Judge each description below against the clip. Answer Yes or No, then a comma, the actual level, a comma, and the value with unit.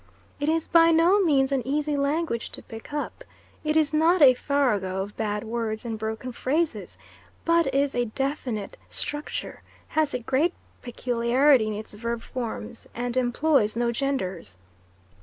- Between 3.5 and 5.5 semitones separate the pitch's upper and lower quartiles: Yes, average, 4.8 semitones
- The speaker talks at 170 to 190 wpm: No, average, 155 wpm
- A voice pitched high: Yes, very high, 255 Hz